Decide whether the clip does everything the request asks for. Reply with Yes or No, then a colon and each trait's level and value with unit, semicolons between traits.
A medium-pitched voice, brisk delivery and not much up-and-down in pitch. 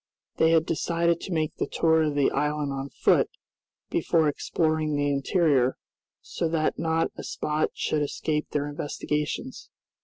No: medium, 155 Hz; average, 150 wpm; narrow, 1.8 semitones